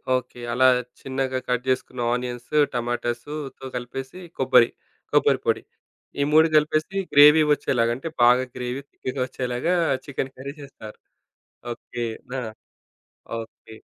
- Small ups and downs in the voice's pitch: Yes, narrow, 2.2 semitones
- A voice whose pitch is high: No, low, 130 Hz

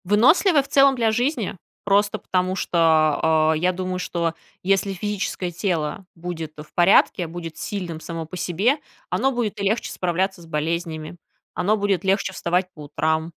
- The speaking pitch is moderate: Yes, medium, 180 Hz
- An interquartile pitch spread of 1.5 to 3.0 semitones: No, average, 3.8 semitones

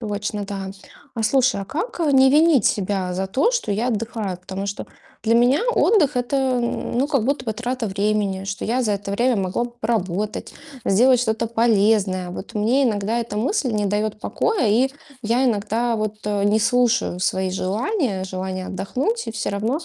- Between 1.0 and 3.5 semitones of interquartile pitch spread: No, average, 3.9 semitones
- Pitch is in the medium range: No, high, 220 Hz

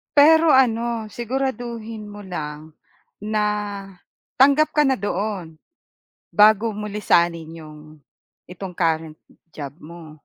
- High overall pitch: Yes, high, 210 Hz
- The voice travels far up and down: Yes, wide, 6.3 semitones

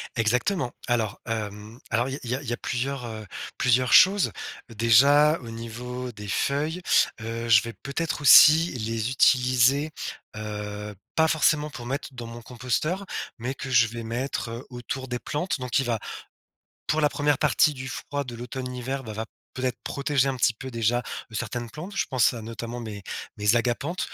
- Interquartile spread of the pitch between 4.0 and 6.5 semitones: No, average, 3.2 semitones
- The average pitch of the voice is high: No, low, 125 Hz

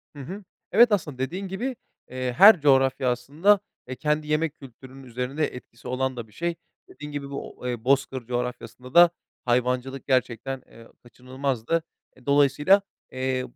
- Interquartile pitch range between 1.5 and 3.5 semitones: Yes, average, 3.2 semitones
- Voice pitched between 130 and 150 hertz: Yes, low, 135 Hz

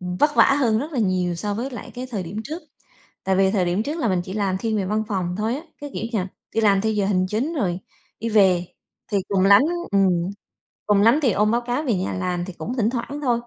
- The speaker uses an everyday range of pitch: Yes, average, 4.1 semitones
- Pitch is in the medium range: No, high, 210 Hz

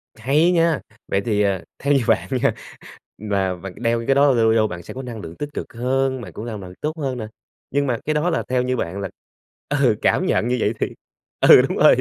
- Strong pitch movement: No, average, 4.9 semitones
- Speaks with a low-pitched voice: Yes, low, 120 Hz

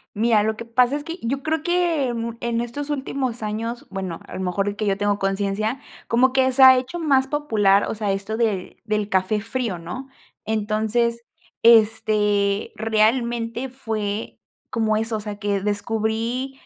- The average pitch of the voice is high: Yes, high, 225 Hz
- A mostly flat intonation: No, average, 3.5 semitones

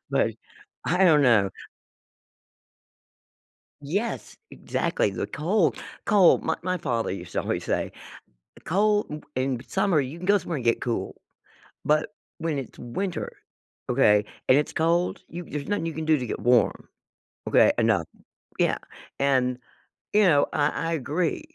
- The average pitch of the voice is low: No, medium, 150 Hz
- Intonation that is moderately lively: No, wide, 5.9 semitones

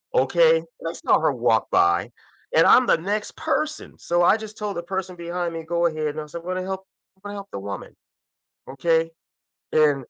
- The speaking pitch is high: No, medium, 175 Hz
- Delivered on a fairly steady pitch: No, average, 4.0 semitones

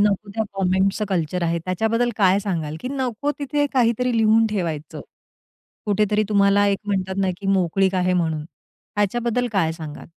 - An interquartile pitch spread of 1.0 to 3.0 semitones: No, average, 3.5 semitones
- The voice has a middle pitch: No, high, 200 Hz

